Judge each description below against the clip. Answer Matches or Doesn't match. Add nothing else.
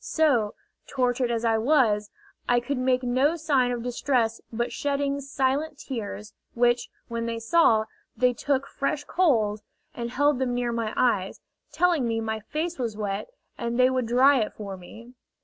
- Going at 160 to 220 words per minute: Matches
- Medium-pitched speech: Doesn't match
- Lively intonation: Doesn't match